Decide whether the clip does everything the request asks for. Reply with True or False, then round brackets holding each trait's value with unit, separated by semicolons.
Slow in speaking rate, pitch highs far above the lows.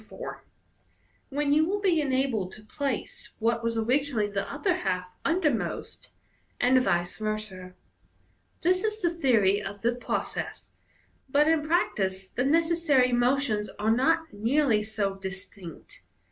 True (130 wpm; 6.4 semitones)